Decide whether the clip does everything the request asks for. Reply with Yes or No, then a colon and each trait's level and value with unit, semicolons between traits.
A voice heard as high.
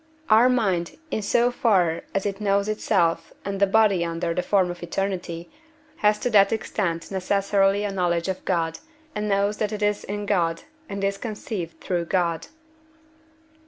Yes: high, 195 Hz